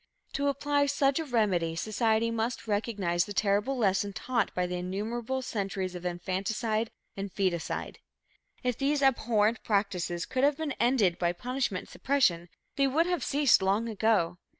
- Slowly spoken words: No, average, 155 wpm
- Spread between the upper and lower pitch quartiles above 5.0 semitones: Yes, wide, 5.5 semitones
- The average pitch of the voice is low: No, high, 220 Hz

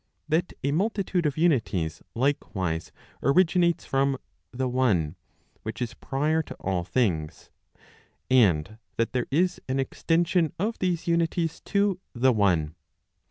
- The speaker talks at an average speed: No, slow, 125 wpm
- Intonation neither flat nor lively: No, wide, 7.7 semitones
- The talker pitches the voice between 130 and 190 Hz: Yes, low, 135 Hz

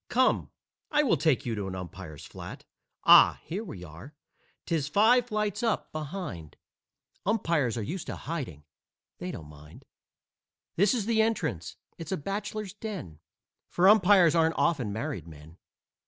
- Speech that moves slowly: No, average, 150 wpm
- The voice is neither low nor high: Yes, medium, 160 Hz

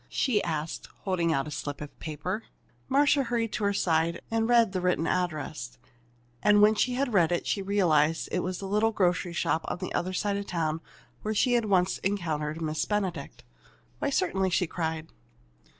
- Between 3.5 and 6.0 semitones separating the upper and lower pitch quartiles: Yes, average, 4.4 semitones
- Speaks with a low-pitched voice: No, medium, 180 Hz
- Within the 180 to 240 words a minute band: Yes, average, 190 wpm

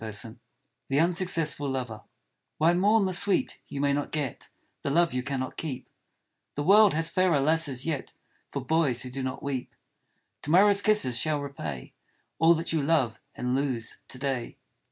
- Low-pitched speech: No, medium, 145 Hz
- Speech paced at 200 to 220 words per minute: No, average, 170 wpm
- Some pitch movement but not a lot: Yes, average, 4.4 semitones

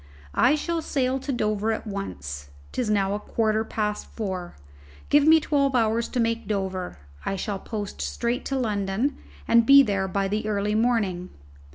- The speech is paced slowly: No, average, 165 wpm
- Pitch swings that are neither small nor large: Yes, average, 4.0 semitones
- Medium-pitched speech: No, high, 215 Hz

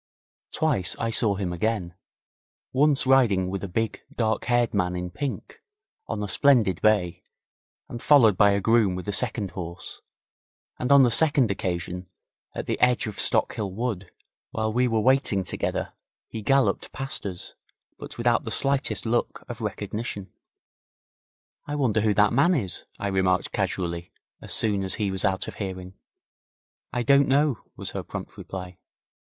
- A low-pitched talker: Yes, low, 110 Hz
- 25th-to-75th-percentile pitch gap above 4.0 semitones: Yes, average, 4.7 semitones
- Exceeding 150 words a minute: Yes, average, 160 wpm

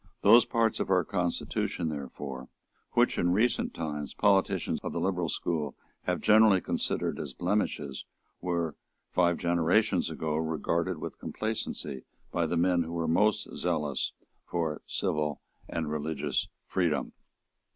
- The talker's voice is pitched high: No, very low, 85 Hz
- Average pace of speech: No, slow, 130 wpm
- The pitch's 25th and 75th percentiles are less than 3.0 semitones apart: No, average, 3.4 semitones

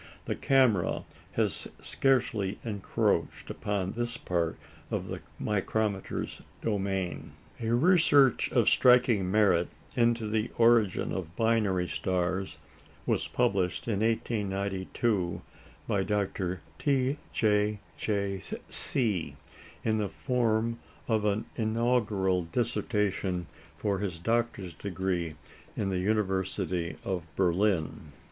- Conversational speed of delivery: No, slow, 105 wpm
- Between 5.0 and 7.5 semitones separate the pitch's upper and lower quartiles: No, average, 3.5 semitones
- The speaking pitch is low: Yes, low, 100 Hz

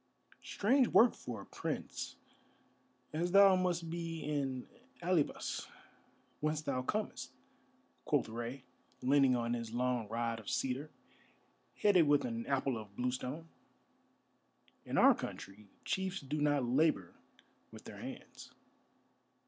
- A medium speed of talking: No, slow, 120 wpm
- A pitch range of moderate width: No, wide, 5.7 semitones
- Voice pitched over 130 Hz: Yes, medium, 140 Hz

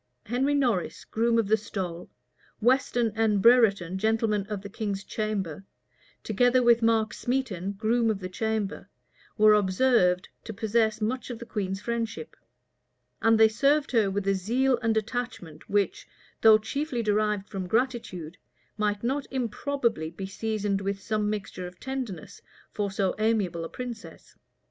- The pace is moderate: Yes, average, 150 wpm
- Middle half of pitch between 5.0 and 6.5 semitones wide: No, average, 3.2 semitones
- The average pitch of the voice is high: Yes, high, 215 Hz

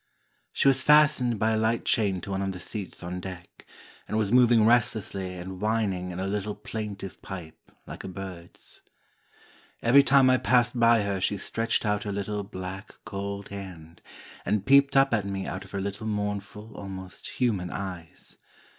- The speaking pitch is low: Yes, low, 100 Hz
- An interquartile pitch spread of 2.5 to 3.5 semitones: Yes, average, 3.1 semitones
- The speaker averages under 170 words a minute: No, average, 175 wpm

